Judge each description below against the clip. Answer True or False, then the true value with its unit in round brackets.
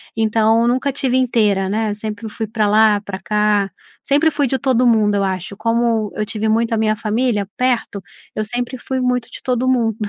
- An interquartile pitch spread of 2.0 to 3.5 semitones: True (2.8 semitones)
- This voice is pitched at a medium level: False (225 Hz)